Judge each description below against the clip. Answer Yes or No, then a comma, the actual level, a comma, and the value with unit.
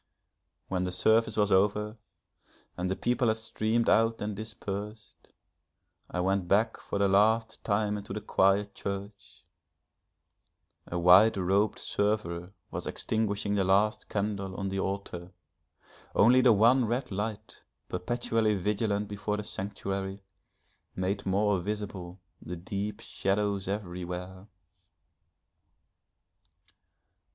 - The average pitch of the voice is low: Yes, low, 100 Hz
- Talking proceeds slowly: Yes, slow, 115 wpm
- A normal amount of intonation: No, narrow, 1.9 semitones